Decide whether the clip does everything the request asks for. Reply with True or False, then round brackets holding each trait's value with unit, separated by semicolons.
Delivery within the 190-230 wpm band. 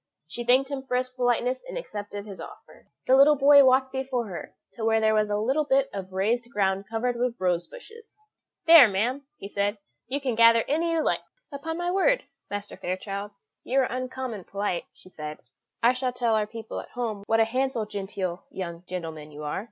True (200 wpm)